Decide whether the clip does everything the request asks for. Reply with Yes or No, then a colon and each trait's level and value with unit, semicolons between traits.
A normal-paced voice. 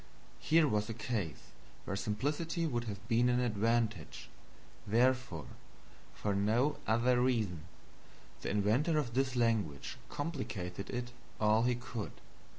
No: slow, 125 wpm